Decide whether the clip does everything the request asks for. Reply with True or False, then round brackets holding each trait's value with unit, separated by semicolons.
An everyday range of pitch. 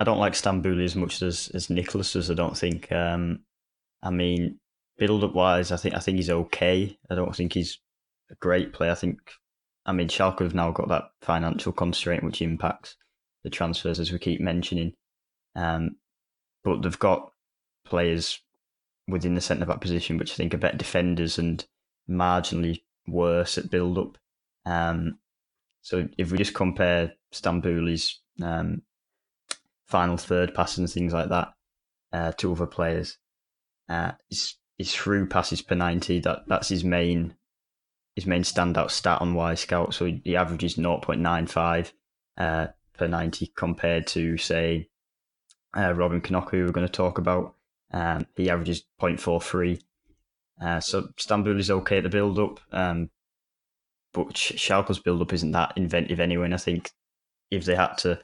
False (1.3 semitones)